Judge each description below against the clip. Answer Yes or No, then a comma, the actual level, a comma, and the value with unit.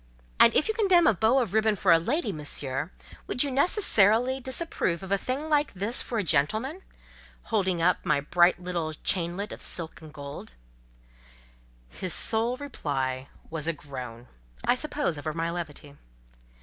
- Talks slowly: No, average, 155 wpm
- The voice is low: No, medium, 185 Hz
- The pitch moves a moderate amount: No, wide, 8.5 semitones